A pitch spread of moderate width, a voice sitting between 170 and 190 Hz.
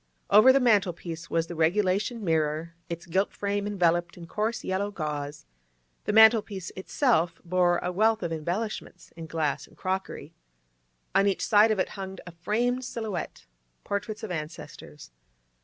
Yes: average, 4.1 semitones; medium, 185 Hz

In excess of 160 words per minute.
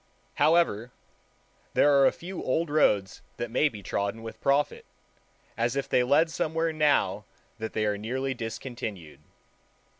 No: average, 145 wpm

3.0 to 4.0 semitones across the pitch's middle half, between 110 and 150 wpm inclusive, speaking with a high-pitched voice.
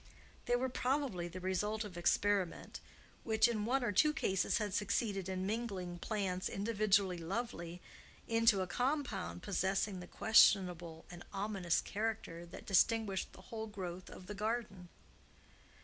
Yes: average, 3.5 semitones; average, 140 wpm; high, 200 Hz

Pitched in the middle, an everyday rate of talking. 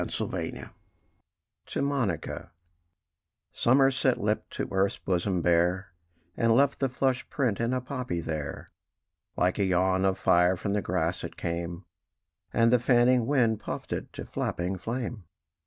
No: low, 100 Hz; average, 150 wpm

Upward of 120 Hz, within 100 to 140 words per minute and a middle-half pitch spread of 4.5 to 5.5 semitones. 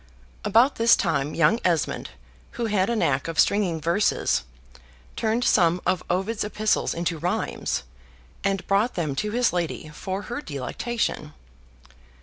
Yes: high, 190 Hz; slow, 135 wpm; average, 5.1 semitones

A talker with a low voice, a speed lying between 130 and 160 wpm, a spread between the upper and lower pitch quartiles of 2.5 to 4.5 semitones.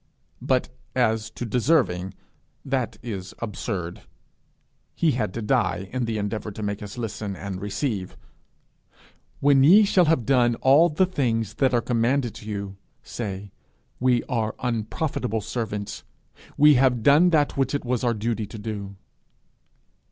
Yes: low, 115 Hz; average, 145 wpm; average, 4.2 semitones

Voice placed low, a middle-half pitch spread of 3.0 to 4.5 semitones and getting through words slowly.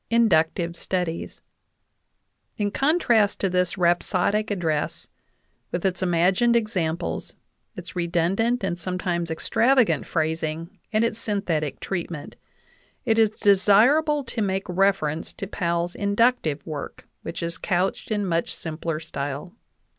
No: medium, 185 Hz; average, 4.0 semitones; slow, 120 wpm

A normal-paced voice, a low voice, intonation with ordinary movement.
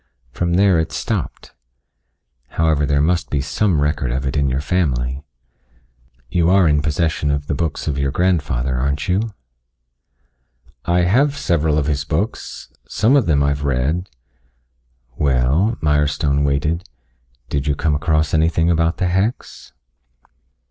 Yes: average, 145 wpm; very low, 75 Hz; average, 3.5 semitones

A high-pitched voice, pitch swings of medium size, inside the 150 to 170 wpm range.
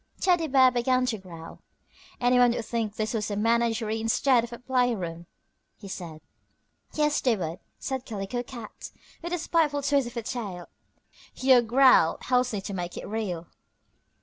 Yes: high, 235 Hz; average, 3.9 semitones; average, 165 wpm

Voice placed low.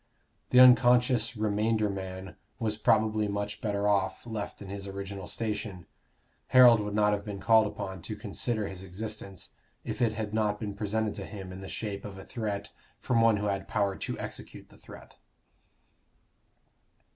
Yes: low, 105 Hz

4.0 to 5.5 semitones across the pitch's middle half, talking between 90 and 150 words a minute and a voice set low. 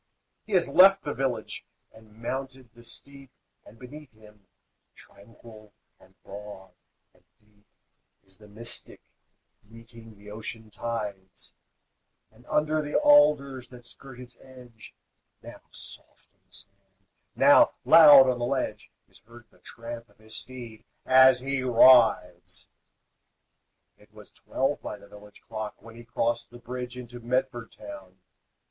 No: average, 3.5 semitones; average, 140 wpm; low, 120 Hz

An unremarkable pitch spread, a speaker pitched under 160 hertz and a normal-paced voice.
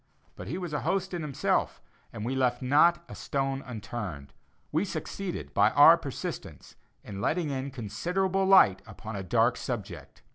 No: wide, 7.4 semitones; low, 135 Hz; average, 160 wpm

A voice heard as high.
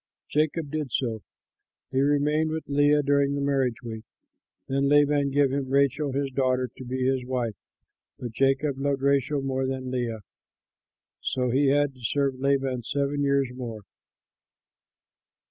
No: low, 135 Hz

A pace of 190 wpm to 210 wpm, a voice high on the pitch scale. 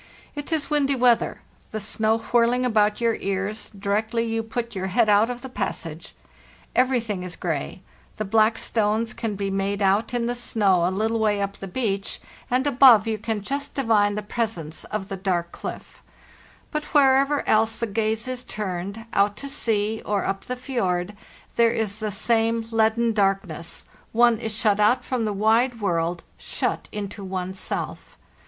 No: average, 175 wpm; high, 220 Hz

